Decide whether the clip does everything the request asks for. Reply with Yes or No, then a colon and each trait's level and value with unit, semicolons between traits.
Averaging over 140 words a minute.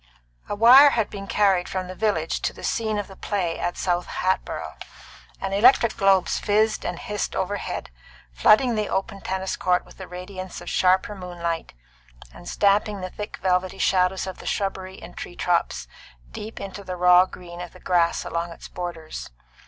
Yes: average, 180 wpm